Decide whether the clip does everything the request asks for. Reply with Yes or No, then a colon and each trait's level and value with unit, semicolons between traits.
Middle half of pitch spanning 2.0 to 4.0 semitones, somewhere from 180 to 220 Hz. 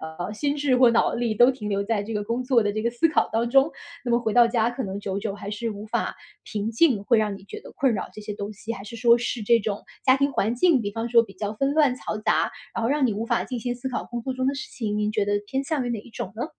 No: average, 3.2 semitones; high, 230 Hz